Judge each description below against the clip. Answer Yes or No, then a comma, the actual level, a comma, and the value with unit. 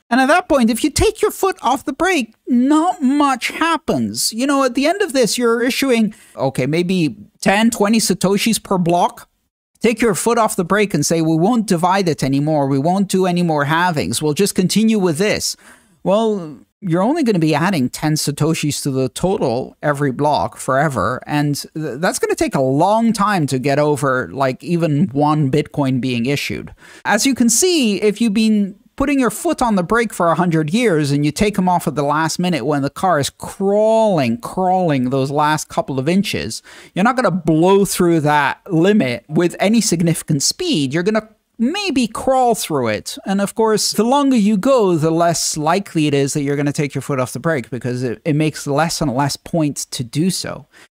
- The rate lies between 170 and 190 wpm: No, fast, 205 wpm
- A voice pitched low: No, medium, 180 Hz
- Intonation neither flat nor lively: No, wide, 7.2 semitones